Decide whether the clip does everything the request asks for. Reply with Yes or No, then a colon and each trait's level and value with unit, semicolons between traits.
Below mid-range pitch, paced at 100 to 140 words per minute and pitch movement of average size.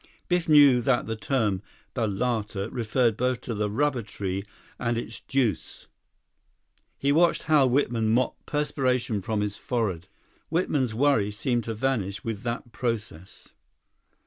Yes: low, 120 Hz; slow, 135 wpm; average, 4.0 semitones